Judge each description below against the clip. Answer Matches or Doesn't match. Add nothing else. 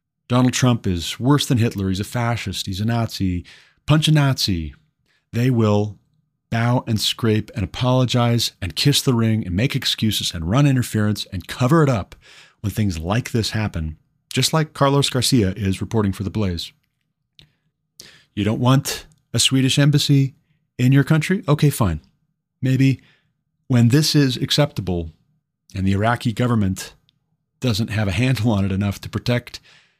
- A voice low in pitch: Matches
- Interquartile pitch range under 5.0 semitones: Doesn't match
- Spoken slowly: Doesn't match